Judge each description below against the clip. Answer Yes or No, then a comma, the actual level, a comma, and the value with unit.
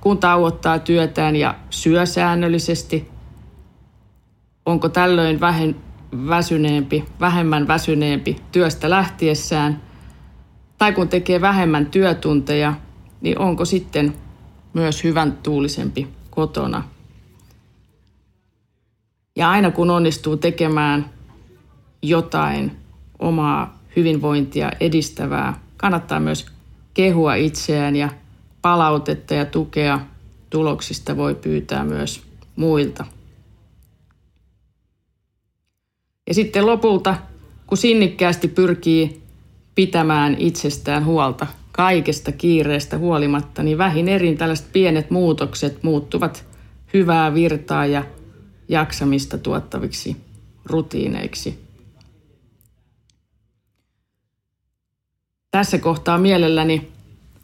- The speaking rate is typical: No, slow, 80 wpm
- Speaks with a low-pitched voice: No, medium, 150 Hz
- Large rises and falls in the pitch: Yes, wide, 7.4 semitones